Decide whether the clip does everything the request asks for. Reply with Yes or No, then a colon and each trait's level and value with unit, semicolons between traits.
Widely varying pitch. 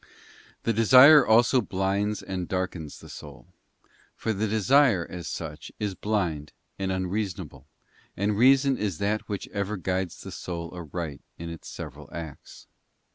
No: average, 3.7 semitones